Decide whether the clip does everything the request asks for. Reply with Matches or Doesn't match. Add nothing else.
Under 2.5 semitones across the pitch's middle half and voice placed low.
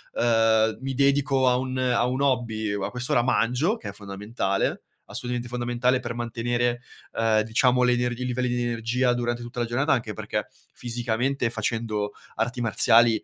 Matches